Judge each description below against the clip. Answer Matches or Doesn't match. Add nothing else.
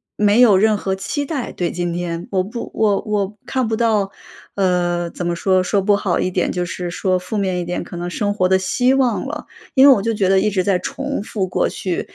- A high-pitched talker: Matches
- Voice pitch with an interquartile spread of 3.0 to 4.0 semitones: Matches